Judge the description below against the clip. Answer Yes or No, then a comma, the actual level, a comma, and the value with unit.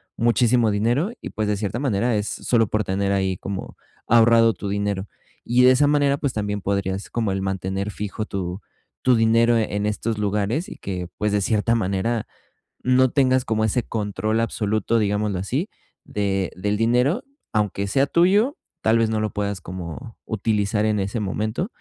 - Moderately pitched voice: No, low, 110 Hz